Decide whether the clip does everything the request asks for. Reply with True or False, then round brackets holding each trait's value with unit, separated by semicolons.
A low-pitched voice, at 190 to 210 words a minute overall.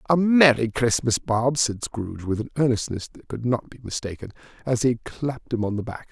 True (120 Hz; 205 wpm)